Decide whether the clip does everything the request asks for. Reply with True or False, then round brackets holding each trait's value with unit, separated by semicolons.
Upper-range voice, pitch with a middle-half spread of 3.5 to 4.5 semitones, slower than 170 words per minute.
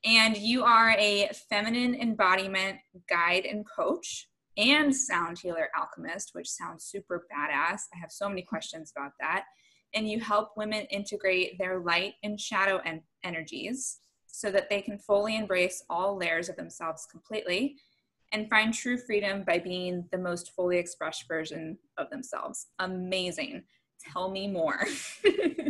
True (200 Hz; 3.9 semitones; 145 wpm)